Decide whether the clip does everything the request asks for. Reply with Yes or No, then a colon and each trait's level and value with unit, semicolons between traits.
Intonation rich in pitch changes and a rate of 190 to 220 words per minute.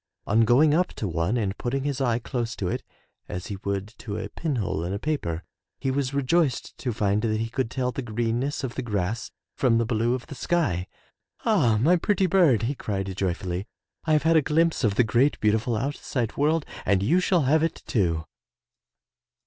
Yes: wide, 5.7 semitones; average, 200 wpm